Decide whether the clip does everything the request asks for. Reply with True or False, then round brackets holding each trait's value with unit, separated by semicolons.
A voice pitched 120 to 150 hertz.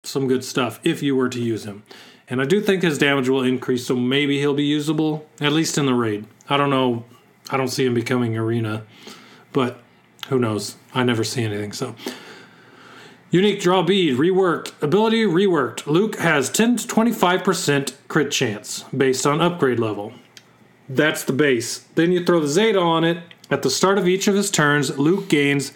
True (140 Hz)